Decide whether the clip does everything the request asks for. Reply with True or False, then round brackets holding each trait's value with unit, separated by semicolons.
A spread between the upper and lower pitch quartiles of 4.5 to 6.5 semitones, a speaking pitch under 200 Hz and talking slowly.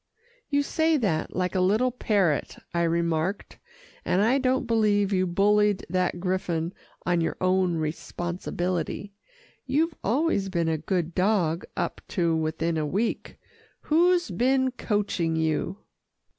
True (5.0 semitones; 185 Hz; 130 wpm)